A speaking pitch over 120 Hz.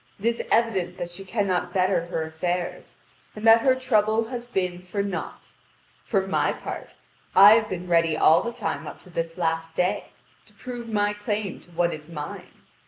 Yes: medium, 185 Hz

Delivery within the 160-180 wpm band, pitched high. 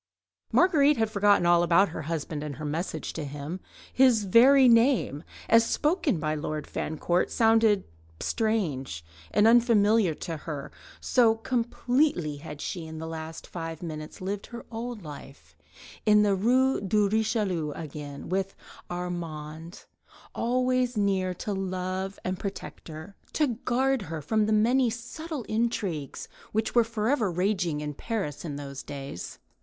No: average, 150 wpm; high, 195 Hz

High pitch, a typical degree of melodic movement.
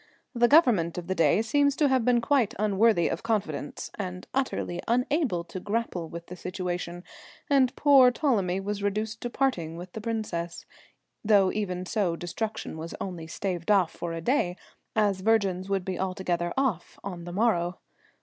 Yes: high, 195 Hz; average, 4.6 semitones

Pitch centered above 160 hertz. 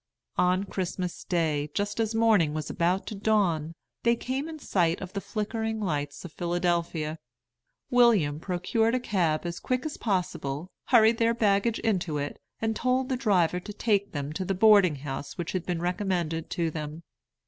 Yes: medium, 185 Hz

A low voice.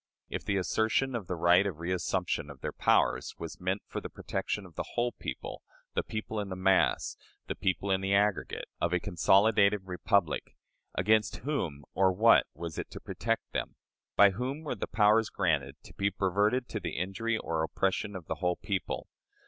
Yes: very low, 95 Hz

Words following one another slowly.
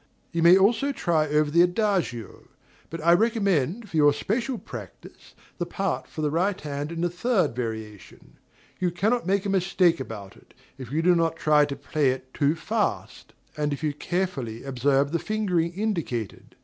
No: average, 175 wpm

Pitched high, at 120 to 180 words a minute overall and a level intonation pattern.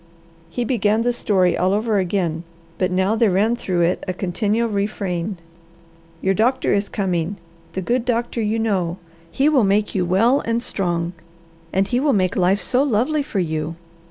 No: high, 200 Hz; average, 175 wpm; average, 4.0 semitones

